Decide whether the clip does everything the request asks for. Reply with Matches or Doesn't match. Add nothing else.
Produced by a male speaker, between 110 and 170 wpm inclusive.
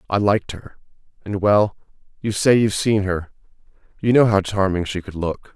Matches